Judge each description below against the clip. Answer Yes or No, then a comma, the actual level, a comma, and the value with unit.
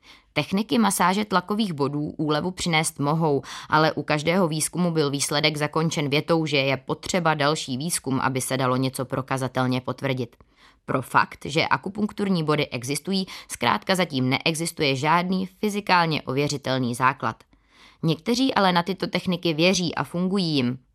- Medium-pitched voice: Yes, medium, 155 Hz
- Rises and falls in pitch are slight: No, average, 4.9 semitones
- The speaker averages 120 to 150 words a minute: Yes, average, 140 wpm